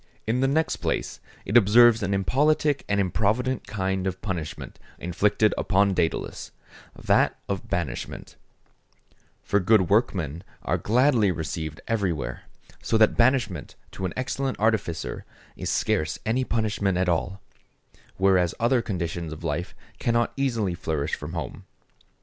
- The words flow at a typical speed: No, slow, 130 wpm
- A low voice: Yes, low, 100 Hz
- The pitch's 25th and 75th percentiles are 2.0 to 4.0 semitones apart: No, average, 5.1 semitones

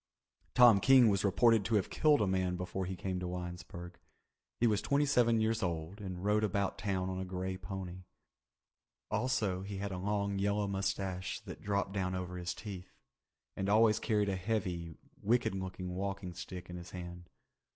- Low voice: Yes, very low, 95 Hz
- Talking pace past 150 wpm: Yes, average, 180 wpm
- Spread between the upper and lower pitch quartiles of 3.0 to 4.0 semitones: No, narrow, 2.4 semitones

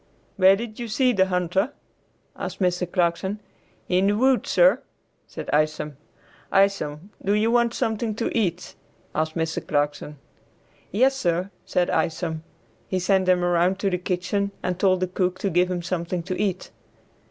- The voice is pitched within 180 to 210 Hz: Yes, medium, 185 Hz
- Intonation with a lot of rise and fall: No, average, 2.7 semitones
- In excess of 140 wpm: Yes, average, 160 wpm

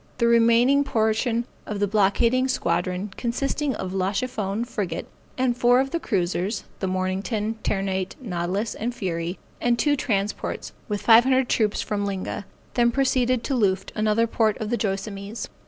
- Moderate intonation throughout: Yes, average, 3.7 semitones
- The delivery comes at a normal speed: Yes, average, 155 wpm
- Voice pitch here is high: Yes, high, 220 Hz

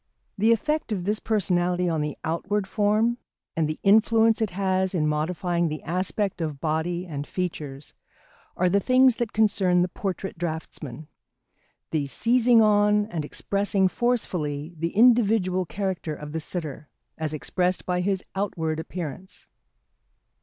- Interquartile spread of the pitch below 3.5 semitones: No, average, 4.5 semitones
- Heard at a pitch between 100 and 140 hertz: No, medium, 180 Hz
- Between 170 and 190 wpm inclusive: No, average, 140 wpm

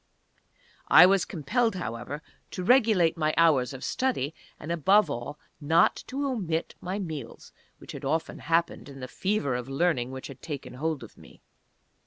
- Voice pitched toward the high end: No, medium, 160 Hz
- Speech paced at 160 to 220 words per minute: Yes, average, 165 wpm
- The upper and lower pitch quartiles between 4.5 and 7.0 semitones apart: Yes, average, 5.3 semitones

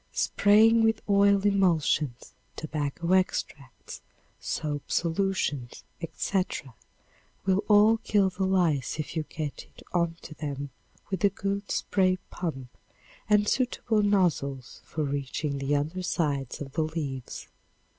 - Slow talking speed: Yes, slow, 120 wpm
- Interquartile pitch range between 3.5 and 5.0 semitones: No, wide, 5.5 semitones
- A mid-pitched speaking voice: Yes, medium, 170 Hz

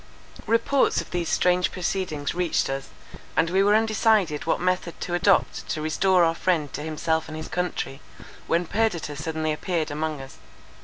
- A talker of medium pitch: Yes, medium, 170 Hz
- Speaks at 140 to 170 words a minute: Yes, average, 165 wpm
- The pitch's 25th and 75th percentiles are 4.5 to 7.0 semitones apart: No, average, 2.9 semitones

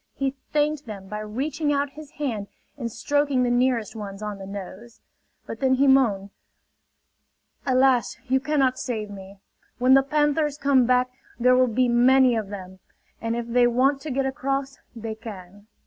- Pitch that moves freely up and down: No, average, 4.1 semitones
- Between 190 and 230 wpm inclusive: No, average, 170 wpm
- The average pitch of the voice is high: Yes, very high, 250 Hz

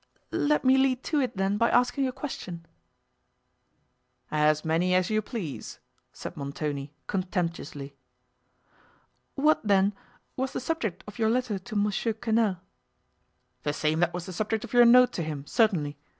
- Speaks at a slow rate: No, average, 150 wpm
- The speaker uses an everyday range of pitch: No, wide, 6.6 semitones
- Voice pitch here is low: No, high, 205 Hz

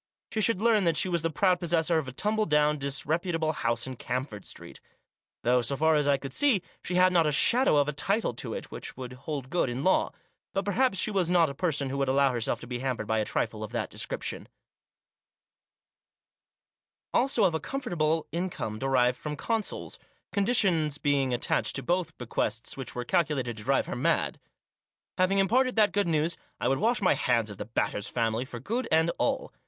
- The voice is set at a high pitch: No, medium, 150 Hz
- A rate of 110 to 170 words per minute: No, fast, 205 wpm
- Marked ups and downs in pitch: Yes, wide, 6.4 semitones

